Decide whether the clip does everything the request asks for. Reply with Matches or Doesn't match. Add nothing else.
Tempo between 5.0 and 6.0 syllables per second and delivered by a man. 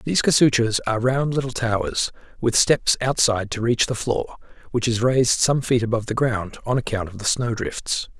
Matches